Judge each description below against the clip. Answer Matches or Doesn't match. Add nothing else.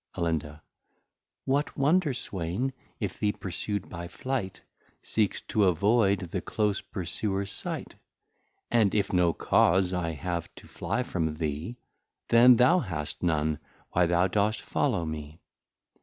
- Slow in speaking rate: Matches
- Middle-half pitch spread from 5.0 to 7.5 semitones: Doesn't match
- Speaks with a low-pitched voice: Matches